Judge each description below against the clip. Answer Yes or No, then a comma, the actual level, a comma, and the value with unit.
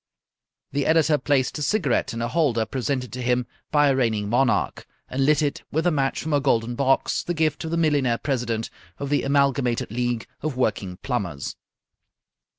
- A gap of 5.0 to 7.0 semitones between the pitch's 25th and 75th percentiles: No, average, 3.5 semitones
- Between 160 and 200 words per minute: Yes, average, 180 wpm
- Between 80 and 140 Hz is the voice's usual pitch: Yes, low, 135 Hz